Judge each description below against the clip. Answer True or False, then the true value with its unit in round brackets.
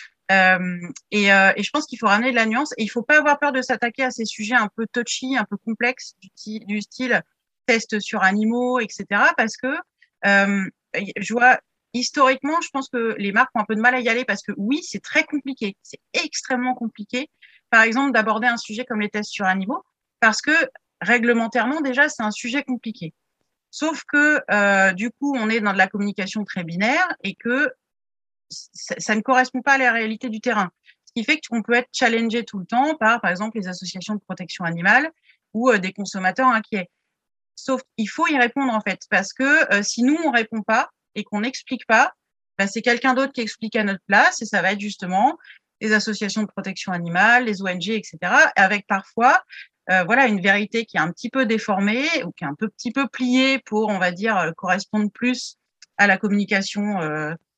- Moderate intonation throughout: True (4.0 semitones)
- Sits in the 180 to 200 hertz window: False (225 Hz)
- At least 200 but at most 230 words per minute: True (215 wpm)